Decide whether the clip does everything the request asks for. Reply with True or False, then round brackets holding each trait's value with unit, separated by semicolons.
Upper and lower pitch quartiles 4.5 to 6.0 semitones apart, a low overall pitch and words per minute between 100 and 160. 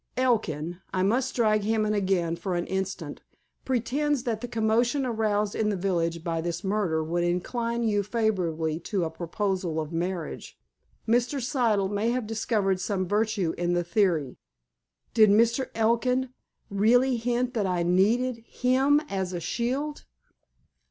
False (5.0 semitones; 210 Hz; 145 wpm)